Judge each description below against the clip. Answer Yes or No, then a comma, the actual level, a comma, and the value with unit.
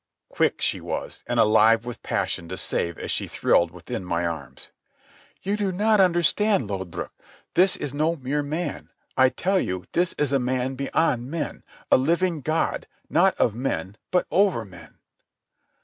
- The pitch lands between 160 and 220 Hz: No, medium, 140 Hz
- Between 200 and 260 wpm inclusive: No, average, 160 wpm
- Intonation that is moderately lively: No, wide, 8.4 semitones